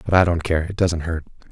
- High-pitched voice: No, very low, 85 Hz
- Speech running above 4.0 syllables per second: Yes, 6.0 syllables/s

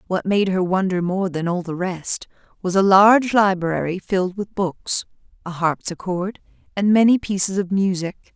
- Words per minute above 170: No, average, 165 wpm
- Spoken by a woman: Yes, female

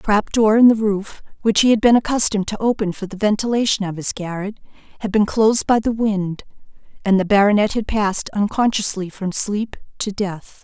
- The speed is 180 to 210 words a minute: Yes, average, 195 wpm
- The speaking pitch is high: Yes, high, 210 Hz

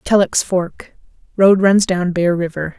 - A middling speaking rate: No, slow, 130 wpm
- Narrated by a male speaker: No, female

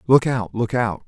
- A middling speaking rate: Yes, average, 170 wpm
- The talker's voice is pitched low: Yes, low, 115 Hz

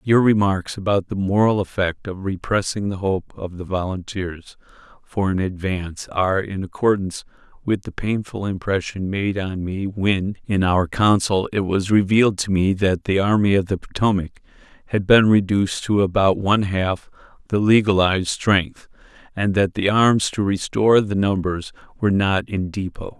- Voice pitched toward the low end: Yes, low, 100 Hz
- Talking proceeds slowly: No, average, 165 wpm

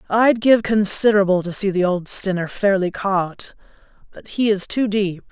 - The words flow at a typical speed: Yes, average, 170 wpm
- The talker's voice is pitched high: Yes, high, 200 Hz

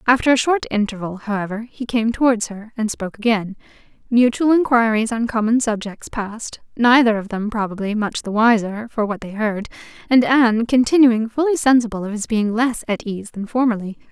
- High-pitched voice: Yes, high, 225 Hz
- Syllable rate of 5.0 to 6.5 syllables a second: Yes, 5.4 syllables/s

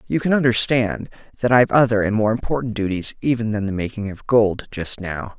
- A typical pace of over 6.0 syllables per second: No, 5.6 syllables/s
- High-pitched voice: No, low, 110 Hz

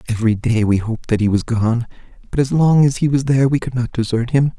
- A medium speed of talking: No, fast, 260 wpm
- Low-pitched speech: Yes, low, 120 Hz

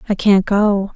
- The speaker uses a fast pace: No, average, 190 wpm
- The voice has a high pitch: Yes, high, 200 Hz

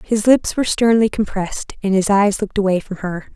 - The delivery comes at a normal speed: No, fast, 215 wpm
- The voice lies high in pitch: Yes, high, 205 Hz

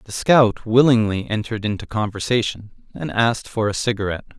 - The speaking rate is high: No, average, 150 wpm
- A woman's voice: No, male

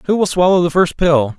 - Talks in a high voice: No, medium, 170 Hz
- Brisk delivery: Yes, fast, 260 wpm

